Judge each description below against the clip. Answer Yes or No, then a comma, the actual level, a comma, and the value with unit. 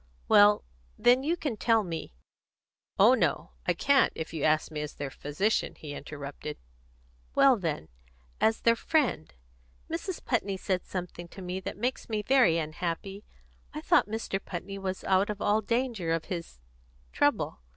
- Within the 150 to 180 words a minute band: Yes, average, 160 wpm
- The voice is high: Yes, high, 195 Hz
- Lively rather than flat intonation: Yes, wide, 5.7 semitones